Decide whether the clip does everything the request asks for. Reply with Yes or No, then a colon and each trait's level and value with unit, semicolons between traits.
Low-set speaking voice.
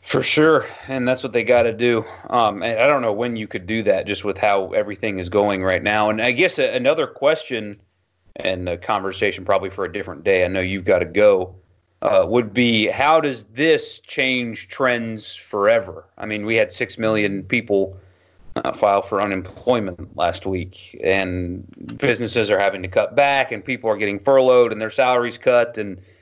Yes: low, 110 Hz